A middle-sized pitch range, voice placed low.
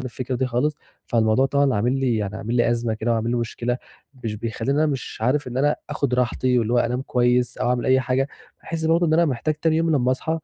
Yes: average, 3.0 semitones; low, 125 Hz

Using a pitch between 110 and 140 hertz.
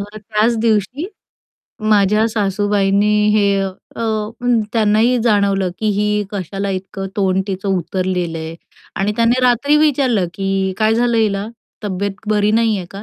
No: high, 205 Hz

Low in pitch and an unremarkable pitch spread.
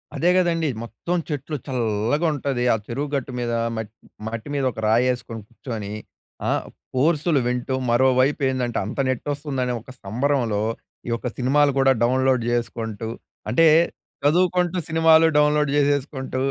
Yes: low, 130 Hz; average, 3.9 semitones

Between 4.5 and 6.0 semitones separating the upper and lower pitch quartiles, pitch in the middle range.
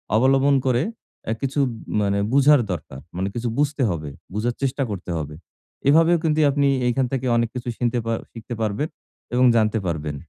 No: average, 5.3 semitones; low, 120 Hz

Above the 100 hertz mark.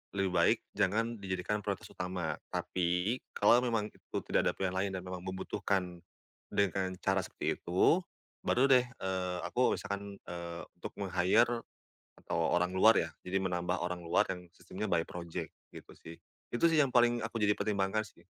No: very low, 95 Hz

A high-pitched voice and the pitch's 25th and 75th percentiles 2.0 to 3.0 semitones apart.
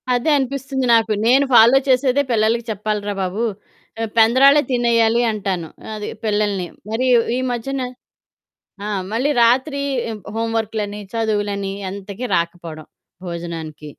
No: high, 220 Hz; average, 3.5 semitones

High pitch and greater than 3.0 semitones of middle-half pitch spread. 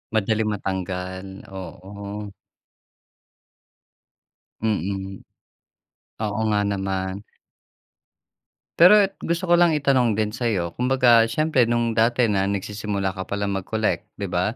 No: low, 105 Hz; average, 3.5 semitones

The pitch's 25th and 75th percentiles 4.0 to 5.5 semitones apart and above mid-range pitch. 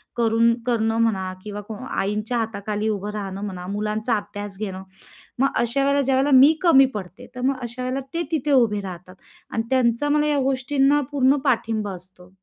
Yes: average, 4.5 semitones; high, 225 Hz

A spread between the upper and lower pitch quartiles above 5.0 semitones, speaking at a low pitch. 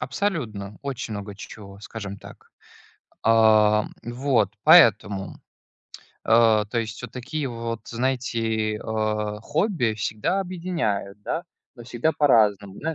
No: average, 3.9 semitones; low, 115 Hz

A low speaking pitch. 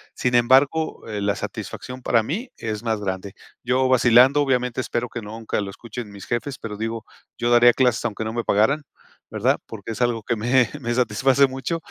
Yes: low, 120 Hz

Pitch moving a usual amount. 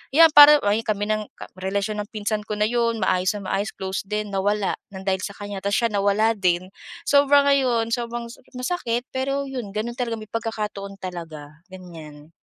Yes: average, 3.4 semitones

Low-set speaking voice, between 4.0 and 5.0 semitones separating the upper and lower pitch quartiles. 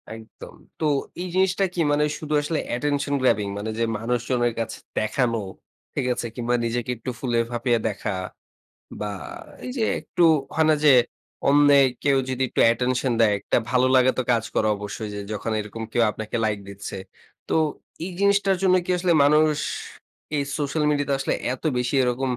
Yes: low, 125 Hz; average, 4.3 semitones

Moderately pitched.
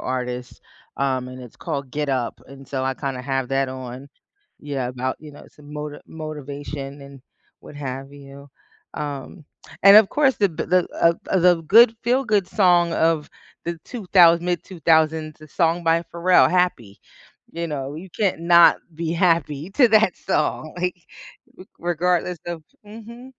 Yes: medium, 155 Hz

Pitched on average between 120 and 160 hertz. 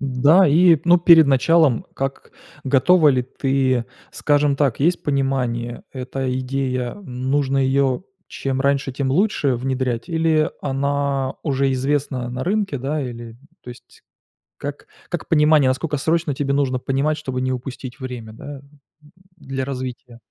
Yes: low, 135 Hz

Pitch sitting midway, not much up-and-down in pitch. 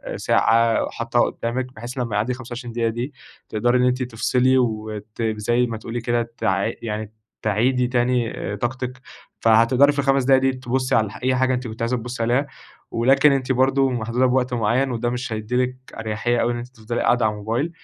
No: low, 120 Hz; narrow, 2.1 semitones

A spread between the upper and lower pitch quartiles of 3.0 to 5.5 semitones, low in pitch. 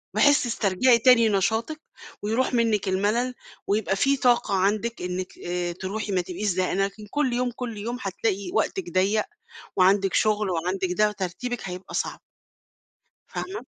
No: average, 4.2 semitones; high, 210 Hz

